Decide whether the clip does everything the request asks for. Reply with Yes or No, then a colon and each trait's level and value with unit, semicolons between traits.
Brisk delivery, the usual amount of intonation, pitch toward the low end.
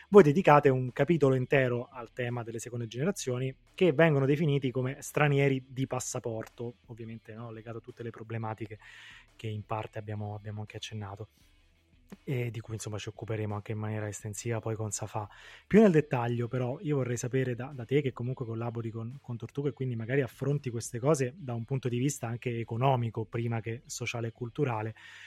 Yes: fast, 185 wpm; average, 3.0 semitones; low, 120 Hz